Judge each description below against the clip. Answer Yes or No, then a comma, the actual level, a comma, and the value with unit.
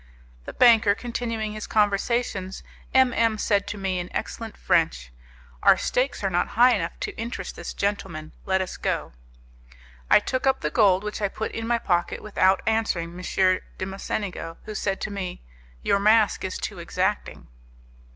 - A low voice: No, high, 205 Hz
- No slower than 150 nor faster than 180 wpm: Yes, average, 170 wpm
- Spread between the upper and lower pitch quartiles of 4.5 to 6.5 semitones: No, average, 3.2 semitones